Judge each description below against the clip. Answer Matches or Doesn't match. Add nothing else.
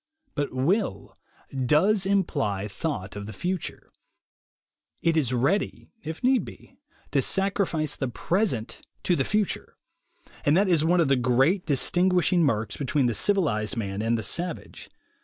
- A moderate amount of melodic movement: Doesn't match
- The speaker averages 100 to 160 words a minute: Matches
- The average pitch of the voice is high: Doesn't match